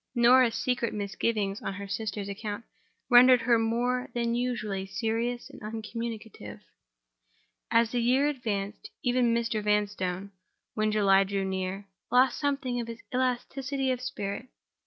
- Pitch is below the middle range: No, high, 230 Hz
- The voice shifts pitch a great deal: No, average, 3.3 semitones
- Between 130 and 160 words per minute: Yes, slow, 135 wpm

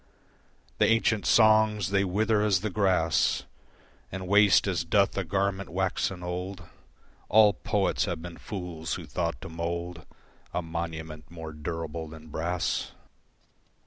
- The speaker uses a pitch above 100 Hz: No, very low, 90 Hz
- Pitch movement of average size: Yes, average, 3.3 semitones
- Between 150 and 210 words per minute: No, slow, 135 wpm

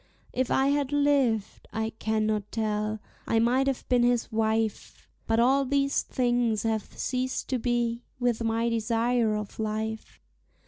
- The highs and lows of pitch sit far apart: No, narrow, 2.4 semitones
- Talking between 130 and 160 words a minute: Yes, average, 145 wpm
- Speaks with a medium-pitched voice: No, high, 230 Hz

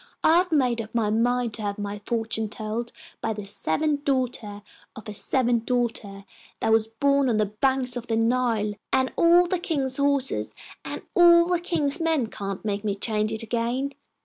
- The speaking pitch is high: Yes, high, 235 Hz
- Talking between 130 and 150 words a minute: No, average, 185 wpm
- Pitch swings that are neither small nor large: Yes, average, 4.4 semitones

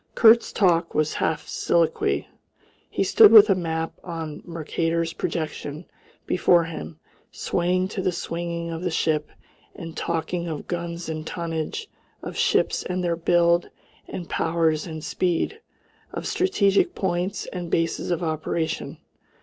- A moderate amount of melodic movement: No, narrow, 1.9 semitones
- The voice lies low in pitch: No, medium, 170 Hz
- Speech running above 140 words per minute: No, slow, 135 wpm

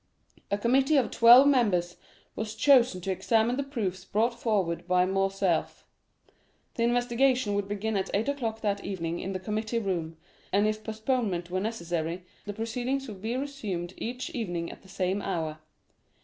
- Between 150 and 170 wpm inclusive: Yes, average, 165 wpm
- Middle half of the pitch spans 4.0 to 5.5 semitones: Yes, average, 4.3 semitones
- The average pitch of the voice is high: Yes, high, 210 Hz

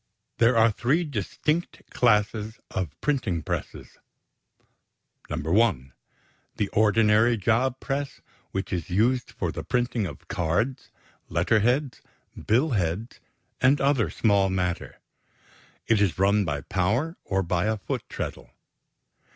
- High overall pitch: No, low, 110 Hz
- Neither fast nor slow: No, slow, 120 wpm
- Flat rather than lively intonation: No, average, 4.7 semitones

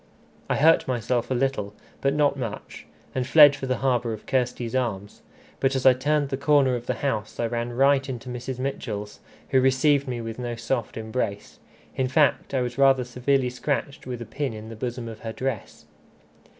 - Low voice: Yes, low, 125 Hz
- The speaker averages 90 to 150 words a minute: No, average, 195 wpm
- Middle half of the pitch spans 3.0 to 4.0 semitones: No, narrow, 2.5 semitones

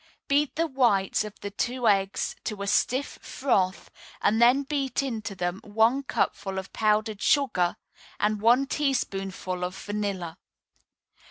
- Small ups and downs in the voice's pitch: No, average, 5.2 semitones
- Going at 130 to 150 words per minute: Yes, average, 140 wpm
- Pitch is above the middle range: Yes, high, 215 Hz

